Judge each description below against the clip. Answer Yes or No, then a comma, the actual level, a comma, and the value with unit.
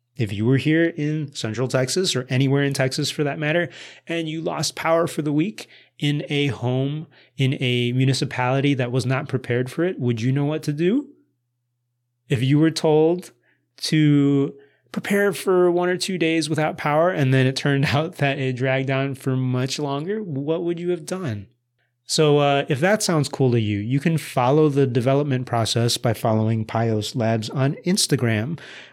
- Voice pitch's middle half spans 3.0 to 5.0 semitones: Yes, average, 3.8 semitones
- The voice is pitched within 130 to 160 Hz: Yes, medium, 140 Hz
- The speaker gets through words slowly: No, average, 185 wpm